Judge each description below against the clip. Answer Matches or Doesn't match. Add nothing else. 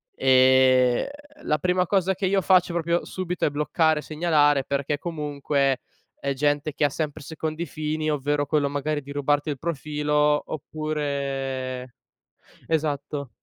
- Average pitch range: Doesn't match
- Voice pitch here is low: Doesn't match